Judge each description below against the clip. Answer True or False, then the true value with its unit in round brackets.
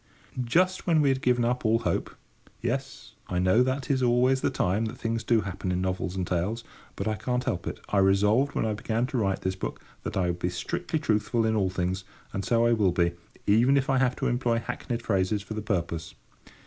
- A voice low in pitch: True (110 Hz)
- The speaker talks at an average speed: False (225 wpm)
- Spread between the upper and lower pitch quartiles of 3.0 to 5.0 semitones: True (4.6 semitones)